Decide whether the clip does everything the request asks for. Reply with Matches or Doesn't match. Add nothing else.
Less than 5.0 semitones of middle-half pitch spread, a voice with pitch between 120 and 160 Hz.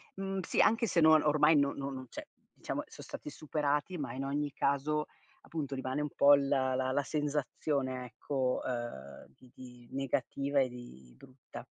Matches